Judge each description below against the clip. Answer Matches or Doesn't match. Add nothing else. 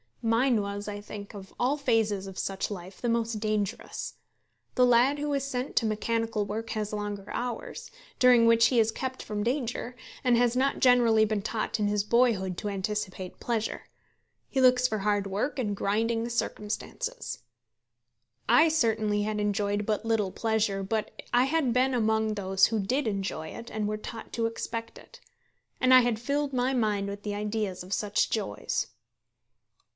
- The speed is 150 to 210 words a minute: Matches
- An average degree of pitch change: Matches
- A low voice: Doesn't match